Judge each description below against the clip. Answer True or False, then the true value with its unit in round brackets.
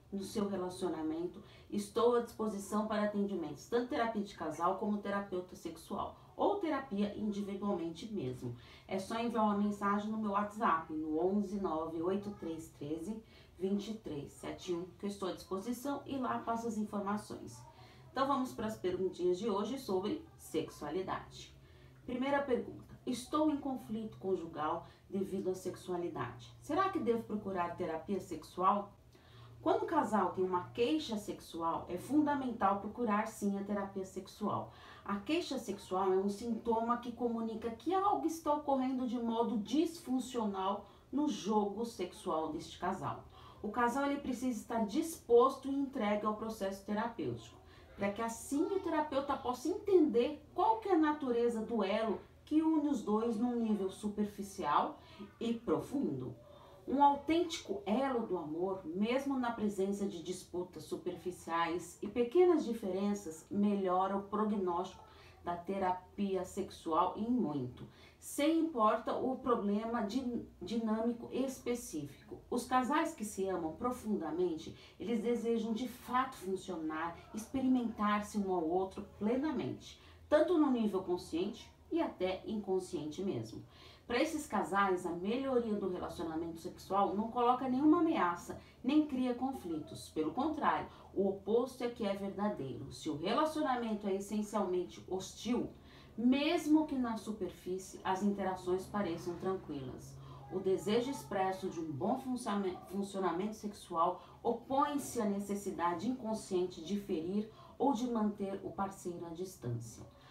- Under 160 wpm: True (130 wpm)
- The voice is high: True (210 Hz)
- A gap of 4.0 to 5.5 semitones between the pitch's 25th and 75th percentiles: True (4.9 semitones)